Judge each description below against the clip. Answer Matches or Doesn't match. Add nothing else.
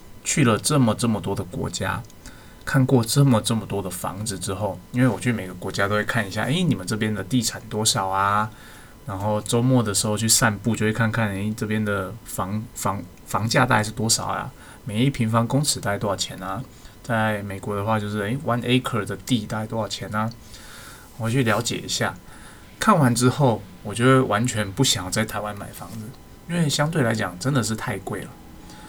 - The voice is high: Doesn't match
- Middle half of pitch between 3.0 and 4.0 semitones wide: Matches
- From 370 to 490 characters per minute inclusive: Doesn't match